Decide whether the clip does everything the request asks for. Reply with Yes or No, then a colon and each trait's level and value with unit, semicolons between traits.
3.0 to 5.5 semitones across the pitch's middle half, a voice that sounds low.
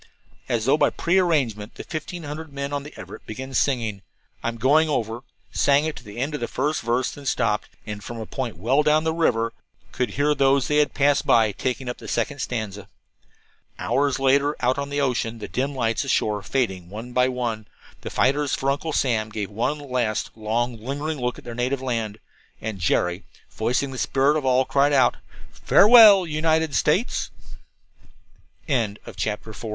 Yes: average, 4.2 semitones; low, 130 Hz